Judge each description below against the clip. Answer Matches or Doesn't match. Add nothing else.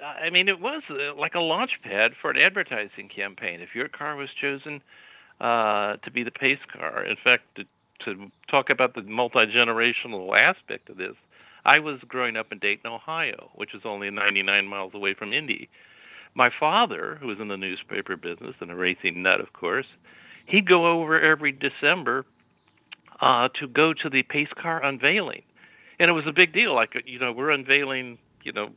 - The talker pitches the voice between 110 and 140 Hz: Matches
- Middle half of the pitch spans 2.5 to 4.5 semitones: Doesn't match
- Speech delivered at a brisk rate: Doesn't match